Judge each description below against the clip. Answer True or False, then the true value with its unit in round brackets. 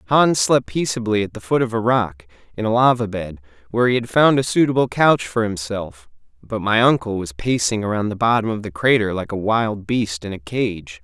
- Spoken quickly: True (215 wpm)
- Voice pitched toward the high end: False (110 Hz)